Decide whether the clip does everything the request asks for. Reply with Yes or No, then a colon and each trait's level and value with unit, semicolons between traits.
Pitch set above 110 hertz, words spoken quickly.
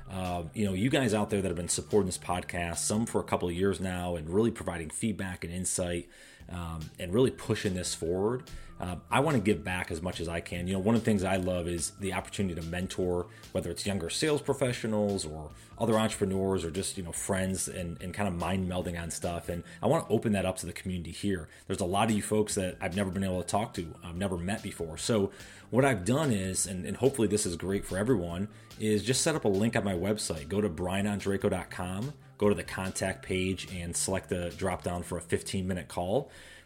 No: very low, 95 Hz; fast, 235 wpm